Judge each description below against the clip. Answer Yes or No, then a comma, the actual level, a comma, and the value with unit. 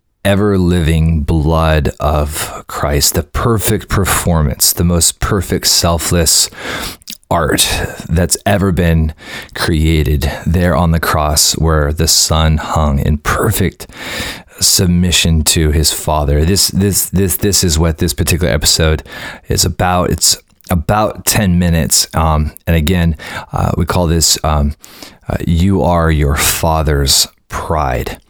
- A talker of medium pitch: No, very low, 85 Hz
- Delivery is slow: Yes, slow, 125 wpm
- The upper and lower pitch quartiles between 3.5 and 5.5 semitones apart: No, average, 2.8 semitones